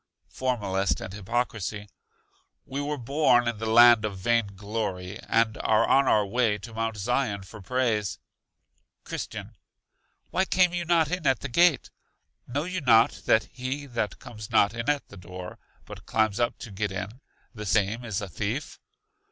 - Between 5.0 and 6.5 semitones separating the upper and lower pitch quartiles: No, average, 4.0 semitones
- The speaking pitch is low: Yes, low, 115 Hz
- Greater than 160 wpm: Yes, average, 170 wpm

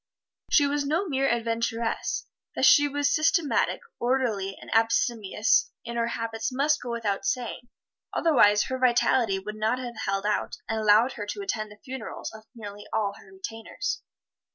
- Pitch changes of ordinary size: Yes, average, 3.8 semitones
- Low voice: No, high, 235 Hz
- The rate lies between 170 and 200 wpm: No, average, 160 wpm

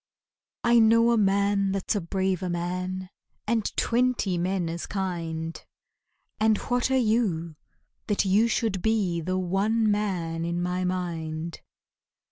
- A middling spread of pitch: Yes, average, 3.8 semitones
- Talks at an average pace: No, slow, 130 wpm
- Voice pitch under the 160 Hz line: No, high, 190 Hz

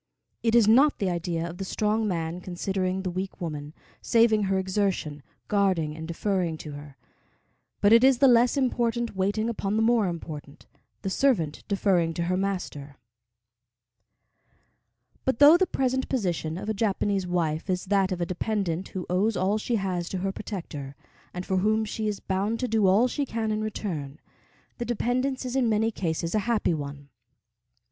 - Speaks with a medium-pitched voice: No, high, 195 Hz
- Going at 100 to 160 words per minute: No, average, 175 wpm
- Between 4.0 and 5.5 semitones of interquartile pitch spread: Yes, average, 4.4 semitones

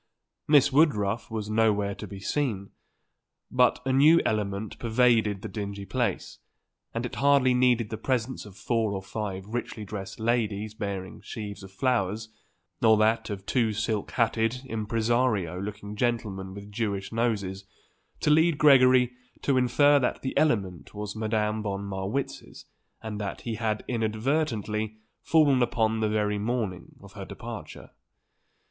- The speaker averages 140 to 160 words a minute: Yes, average, 145 wpm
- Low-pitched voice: Yes, low, 110 Hz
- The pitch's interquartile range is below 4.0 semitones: Yes, average, 3.3 semitones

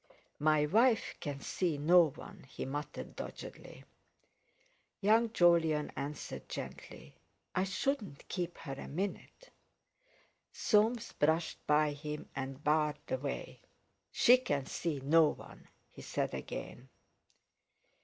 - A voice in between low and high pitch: Yes, medium, 155 Hz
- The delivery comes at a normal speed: No, slow, 115 wpm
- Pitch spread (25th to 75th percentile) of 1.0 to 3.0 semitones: No, average, 4.9 semitones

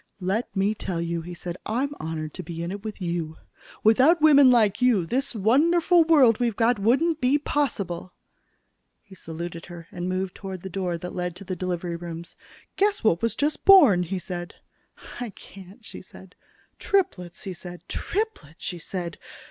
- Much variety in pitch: Yes, wide, 6.2 semitones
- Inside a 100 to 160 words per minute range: No, average, 175 wpm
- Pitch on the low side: No, high, 190 Hz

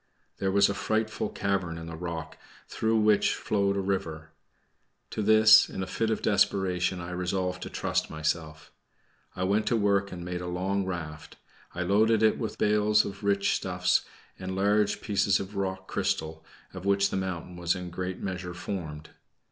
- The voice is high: No, very low, 95 Hz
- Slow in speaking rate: No, average, 180 wpm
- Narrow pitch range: Yes, narrow, 2.3 semitones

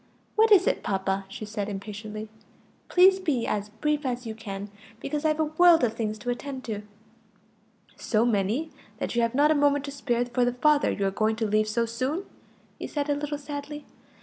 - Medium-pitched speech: No, high, 245 Hz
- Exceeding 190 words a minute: Yes, average, 200 wpm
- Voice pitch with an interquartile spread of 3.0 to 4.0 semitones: No, wide, 5.6 semitones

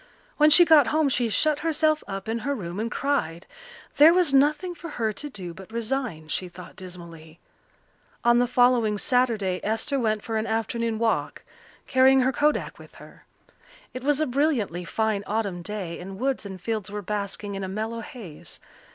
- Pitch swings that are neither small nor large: No, wide, 5.7 semitones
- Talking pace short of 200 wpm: Yes, average, 180 wpm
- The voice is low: No, high, 225 Hz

